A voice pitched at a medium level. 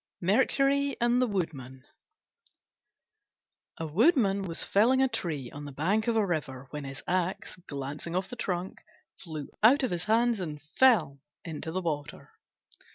Yes: medium, 180 Hz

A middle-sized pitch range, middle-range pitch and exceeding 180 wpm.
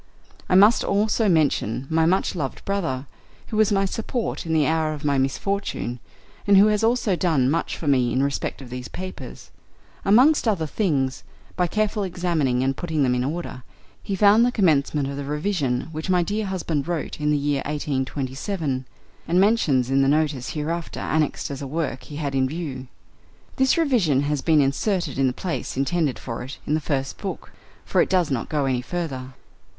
No: wide, 5.7 semitones; medium, 155 Hz; average, 190 wpm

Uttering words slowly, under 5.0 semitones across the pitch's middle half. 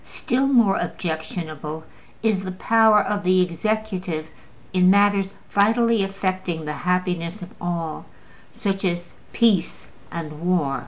Yes: slow, 120 wpm; average, 3.4 semitones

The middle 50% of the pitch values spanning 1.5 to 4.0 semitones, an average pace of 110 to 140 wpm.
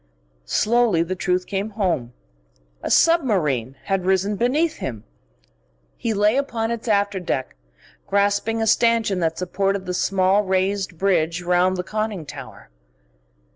Yes: average, 3.3 semitones; slow, 135 wpm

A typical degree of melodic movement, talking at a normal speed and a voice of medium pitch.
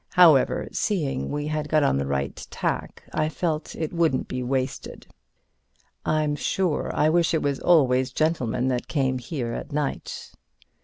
Yes: average, 3.4 semitones; average, 165 wpm; medium, 145 Hz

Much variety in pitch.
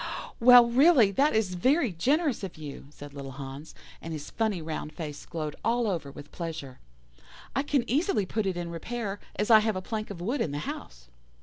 Yes: wide, 7.4 semitones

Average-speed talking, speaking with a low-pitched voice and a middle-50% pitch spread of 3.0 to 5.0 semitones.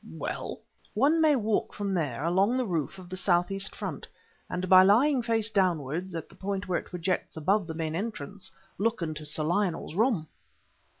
No: average, 180 wpm; high, 190 Hz; average, 4.1 semitones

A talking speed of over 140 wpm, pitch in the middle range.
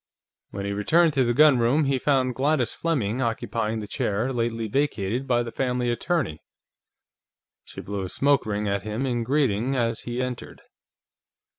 No: average, 160 wpm; low, 120 Hz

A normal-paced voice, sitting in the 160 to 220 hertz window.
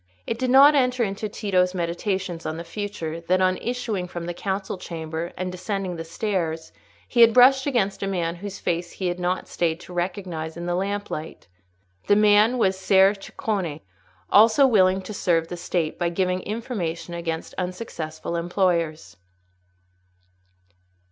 Yes: average, 155 wpm; medium, 185 Hz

